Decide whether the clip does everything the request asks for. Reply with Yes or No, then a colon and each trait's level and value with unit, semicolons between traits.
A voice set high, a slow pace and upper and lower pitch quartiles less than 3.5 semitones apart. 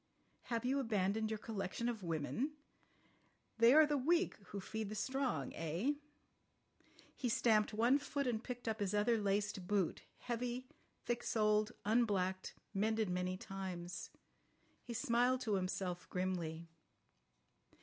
No: high, 215 Hz; slow, 130 wpm; average, 4.3 semitones